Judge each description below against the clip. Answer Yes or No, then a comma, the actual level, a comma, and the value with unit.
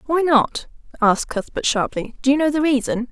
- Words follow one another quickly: No, average, 195 wpm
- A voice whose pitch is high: Yes, very high, 270 Hz